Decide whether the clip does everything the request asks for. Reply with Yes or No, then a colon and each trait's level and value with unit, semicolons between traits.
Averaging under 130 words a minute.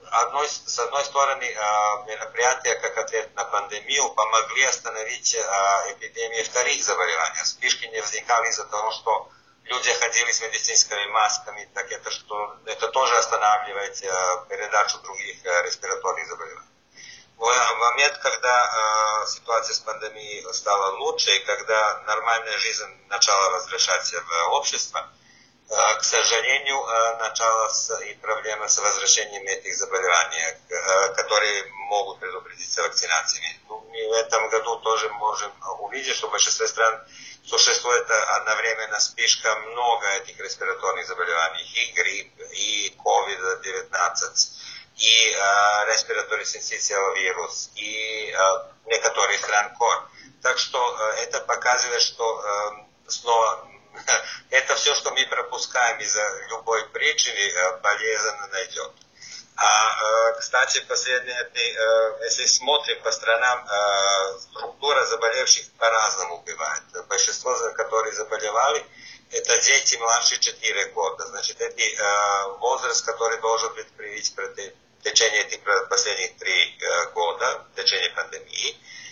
Yes: slow, 110 wpm